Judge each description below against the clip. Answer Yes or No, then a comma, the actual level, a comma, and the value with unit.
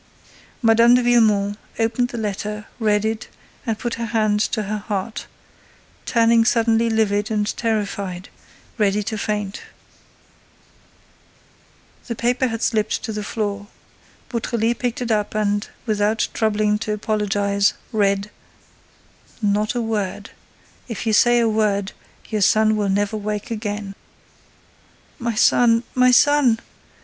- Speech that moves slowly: Yes, slow, 125 wpm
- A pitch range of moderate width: No, narrow, 1.8 semitones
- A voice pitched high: Yes, high, 215 Hz